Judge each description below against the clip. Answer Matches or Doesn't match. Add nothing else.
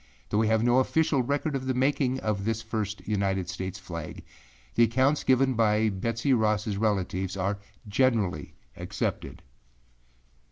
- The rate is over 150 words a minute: Doesn't match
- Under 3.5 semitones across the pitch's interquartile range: Doesn't match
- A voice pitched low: Matches